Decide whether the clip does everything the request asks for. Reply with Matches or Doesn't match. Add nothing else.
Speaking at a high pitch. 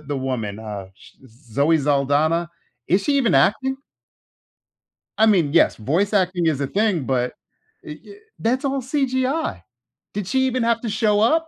Doesn't match